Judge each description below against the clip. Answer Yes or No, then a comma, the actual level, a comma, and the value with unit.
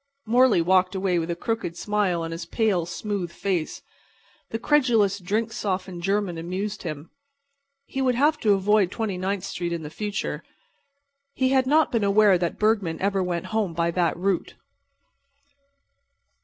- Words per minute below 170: Yes, average, 155 wpm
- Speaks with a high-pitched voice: Yes, high, 195 Hz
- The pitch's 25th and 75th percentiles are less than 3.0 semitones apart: No, average, 3.8 semitones